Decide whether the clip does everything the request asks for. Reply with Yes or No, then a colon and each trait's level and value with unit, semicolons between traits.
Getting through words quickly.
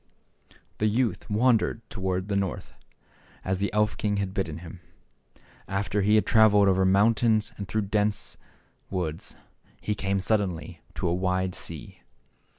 No: average, 150 wpm